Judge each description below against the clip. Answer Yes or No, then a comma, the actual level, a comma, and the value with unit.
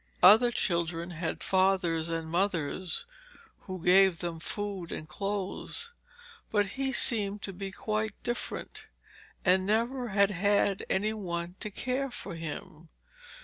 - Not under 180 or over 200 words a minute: No, slow, 135 wpm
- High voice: Yes, high, 195 Hz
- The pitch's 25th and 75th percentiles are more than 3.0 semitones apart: Yes, average, 3.6 semitones